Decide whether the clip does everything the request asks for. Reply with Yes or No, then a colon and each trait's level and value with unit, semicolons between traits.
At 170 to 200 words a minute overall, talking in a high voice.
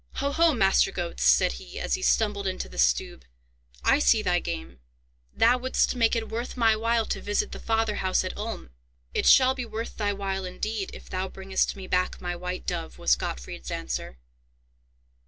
Yes: average, 190 wpm; high, 200 Hz